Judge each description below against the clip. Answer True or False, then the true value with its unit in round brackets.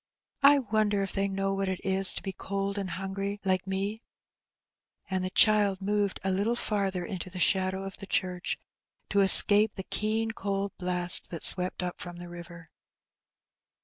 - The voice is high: True (195 Hz)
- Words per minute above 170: True (180 wpm)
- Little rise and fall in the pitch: True (1.5 semitones)